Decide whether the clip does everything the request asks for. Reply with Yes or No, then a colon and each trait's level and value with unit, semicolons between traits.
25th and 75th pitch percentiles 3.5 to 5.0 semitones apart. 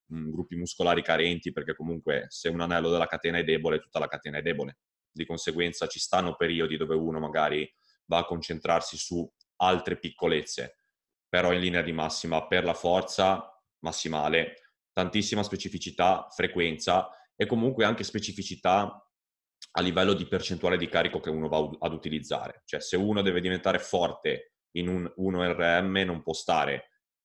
No: narrow, 2.5 semitones